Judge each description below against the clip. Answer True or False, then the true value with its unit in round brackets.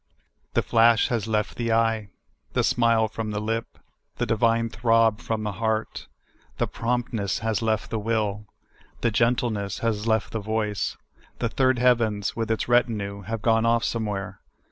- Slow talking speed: False (160 wpm)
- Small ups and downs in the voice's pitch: True (1.5 semitones)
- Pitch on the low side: True (115 Hz)